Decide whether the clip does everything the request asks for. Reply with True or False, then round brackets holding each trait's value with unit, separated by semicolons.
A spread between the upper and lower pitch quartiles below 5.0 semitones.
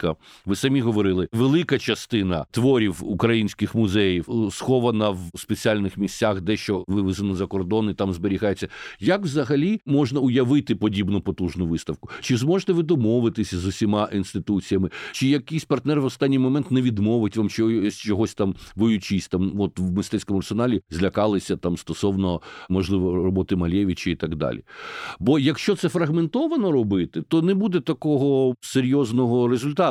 False (5.5 semitones)